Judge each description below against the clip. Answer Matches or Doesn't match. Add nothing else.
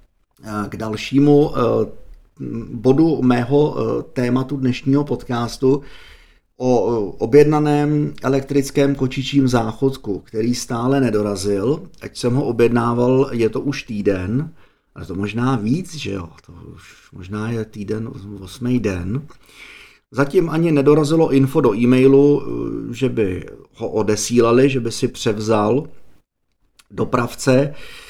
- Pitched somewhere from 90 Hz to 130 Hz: Matches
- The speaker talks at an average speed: Doesn't match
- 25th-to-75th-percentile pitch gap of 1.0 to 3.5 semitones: Doesn't match